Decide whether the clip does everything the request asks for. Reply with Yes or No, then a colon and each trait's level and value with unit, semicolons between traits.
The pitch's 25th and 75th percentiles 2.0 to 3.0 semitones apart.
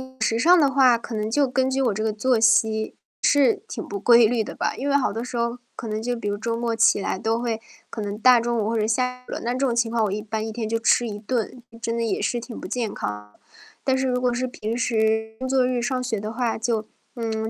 Yes: narrow, 2.4 semitones